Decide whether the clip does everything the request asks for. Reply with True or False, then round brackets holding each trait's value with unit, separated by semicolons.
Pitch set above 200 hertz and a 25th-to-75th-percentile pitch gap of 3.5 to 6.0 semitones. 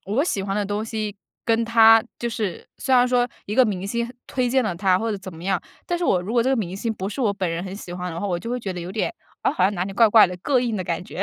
True (210 Hz; 3.9 semitones)